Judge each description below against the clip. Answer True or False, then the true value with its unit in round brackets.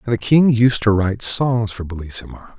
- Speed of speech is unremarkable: False (210 wpm)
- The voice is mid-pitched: False (110 Hz)